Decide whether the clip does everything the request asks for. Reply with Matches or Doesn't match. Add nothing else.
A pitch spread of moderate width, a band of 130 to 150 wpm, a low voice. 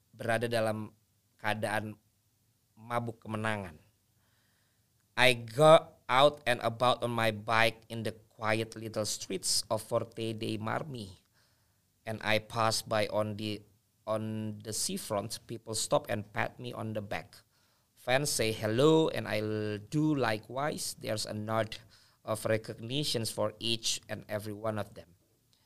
Doesn't match